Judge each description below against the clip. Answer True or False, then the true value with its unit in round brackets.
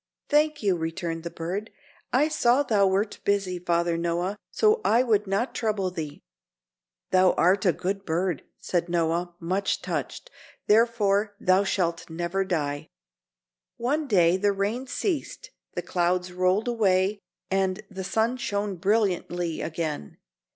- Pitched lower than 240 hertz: True (190 Hz)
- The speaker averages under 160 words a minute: True (135 wpm)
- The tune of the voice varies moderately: True (3.6 semitones)